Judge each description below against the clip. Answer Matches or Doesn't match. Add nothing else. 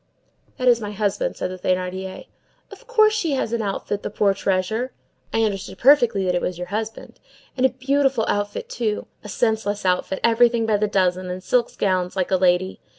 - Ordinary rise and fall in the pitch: Matches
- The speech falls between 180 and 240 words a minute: Matches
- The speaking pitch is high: Matches